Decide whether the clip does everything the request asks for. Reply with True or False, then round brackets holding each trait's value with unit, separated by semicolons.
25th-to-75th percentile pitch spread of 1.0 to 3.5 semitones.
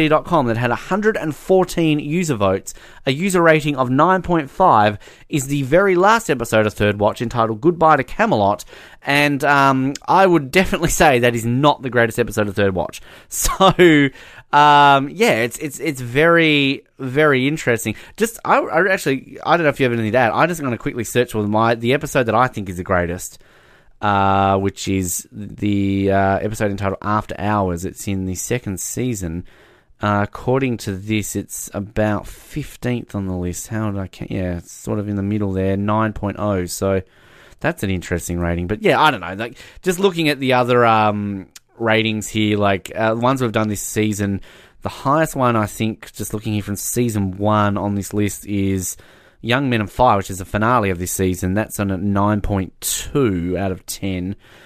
False (5.5 semitones)